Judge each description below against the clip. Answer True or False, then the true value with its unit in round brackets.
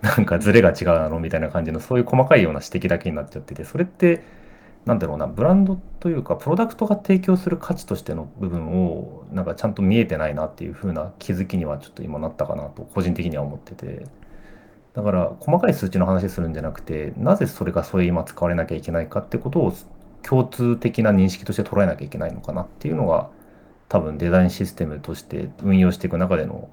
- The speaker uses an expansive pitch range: True (6.3 semitones)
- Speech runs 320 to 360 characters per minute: False (475 characters per minute)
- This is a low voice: True (95 Hz)